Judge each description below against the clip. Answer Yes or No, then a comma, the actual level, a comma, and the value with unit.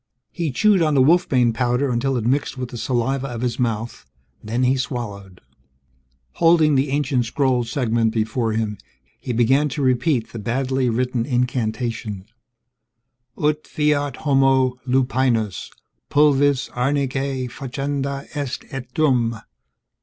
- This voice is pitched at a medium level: No, low, 130 Hz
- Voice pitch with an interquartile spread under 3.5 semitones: Yes, average, 2.8 semitones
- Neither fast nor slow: No, slow, 130 wpm